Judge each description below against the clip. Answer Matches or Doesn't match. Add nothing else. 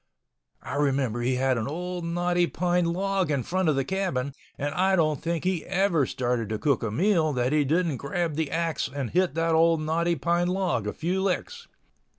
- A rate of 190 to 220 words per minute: Matches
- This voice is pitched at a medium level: Matches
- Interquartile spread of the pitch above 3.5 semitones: Matches